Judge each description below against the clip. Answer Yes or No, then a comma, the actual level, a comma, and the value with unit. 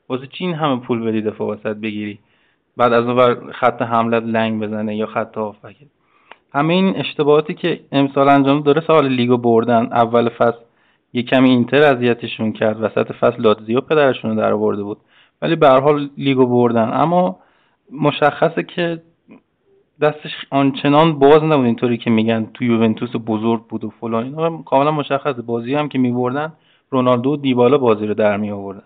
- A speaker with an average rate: No, fast, 160 wpm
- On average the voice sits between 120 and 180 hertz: Yes, low, 125 Hz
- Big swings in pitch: No, average, 4.2 semitones